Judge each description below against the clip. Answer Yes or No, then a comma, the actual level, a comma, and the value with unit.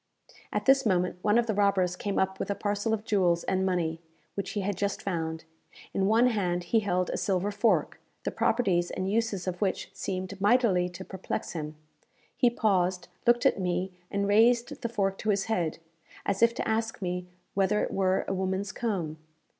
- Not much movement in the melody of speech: No, average, 3.0 semitones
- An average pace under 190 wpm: No, average, 195 wpm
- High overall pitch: Yes, high, 195 Hz